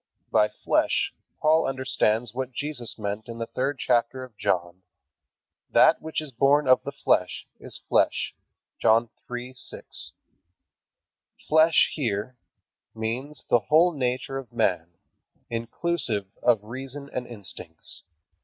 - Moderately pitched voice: No, low, 125 Hz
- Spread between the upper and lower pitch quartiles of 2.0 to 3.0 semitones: No, average, 3.8 semitones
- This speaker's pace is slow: Yes, slow, 120 wpm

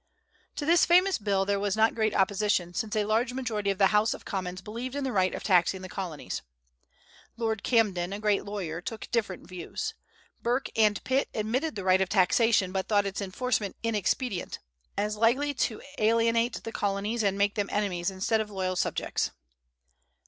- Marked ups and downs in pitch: No, average, 3.1 semitones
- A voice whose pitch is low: No, high, 210 Hz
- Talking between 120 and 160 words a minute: No, average, 180 wpm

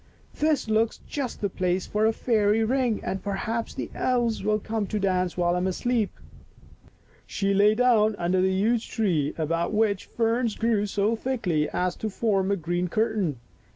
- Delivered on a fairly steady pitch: No, average, 3.5 semitones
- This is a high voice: Yes, high, 210 Hz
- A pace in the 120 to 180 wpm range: Yes, average, 175 wpm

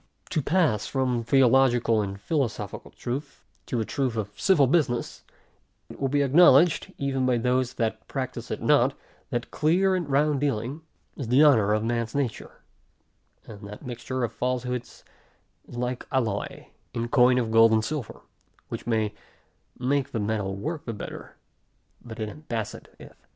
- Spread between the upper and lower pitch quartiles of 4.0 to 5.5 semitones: No, average, 3.6 semitones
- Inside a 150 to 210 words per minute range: Yes, average, 155 wpm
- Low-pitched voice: Yes, low, 125 Hz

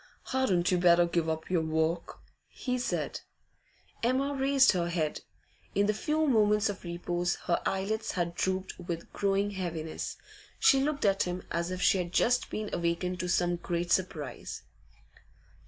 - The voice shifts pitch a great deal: No, average, 3.6 semitones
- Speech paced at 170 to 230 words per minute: No, average, 155 wpm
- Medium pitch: Yes, medium, 180 Hz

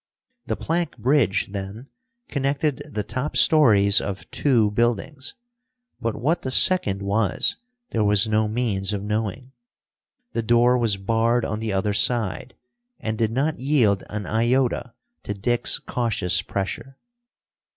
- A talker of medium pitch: No, low, 115 Hz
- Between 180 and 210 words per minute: No, slow, 135 wpm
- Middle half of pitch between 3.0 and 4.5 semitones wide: Yes, average, 3.8 semitones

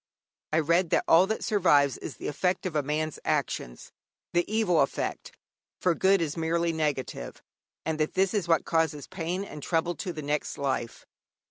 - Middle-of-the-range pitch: Yes, medium, 165 Hz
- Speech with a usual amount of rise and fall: Yes, average, 3.2 semitones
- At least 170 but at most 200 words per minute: Yes, average, 175 wpm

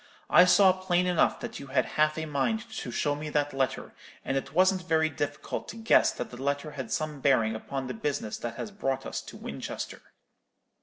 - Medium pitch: Yes, medium, 145 Hz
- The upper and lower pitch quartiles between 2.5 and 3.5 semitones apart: No, average, 4.9 semitones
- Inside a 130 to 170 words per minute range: No, fast, 205 wpm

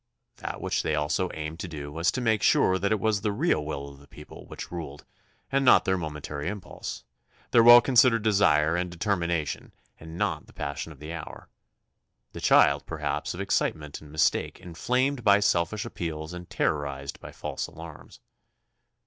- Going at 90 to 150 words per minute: No, average, 175 wpm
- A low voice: Yes, very low, 85 Hz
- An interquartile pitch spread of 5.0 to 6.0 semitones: Yes, average, 5.3 semitones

